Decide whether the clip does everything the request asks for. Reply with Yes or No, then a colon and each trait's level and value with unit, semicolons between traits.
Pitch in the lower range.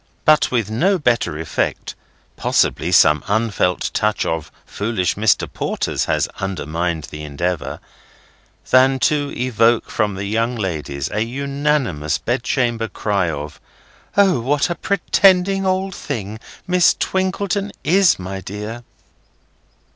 Yes: low, 115 Hz